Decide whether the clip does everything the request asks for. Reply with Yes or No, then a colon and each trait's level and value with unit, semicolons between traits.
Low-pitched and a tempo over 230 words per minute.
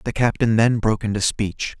No: low, 110 Hz; average, 200 wpm